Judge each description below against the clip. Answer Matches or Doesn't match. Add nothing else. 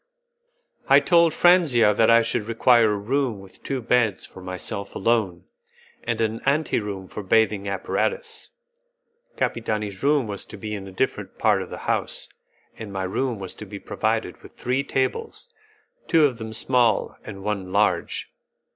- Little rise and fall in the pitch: Doesn't match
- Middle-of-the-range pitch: Doesn't match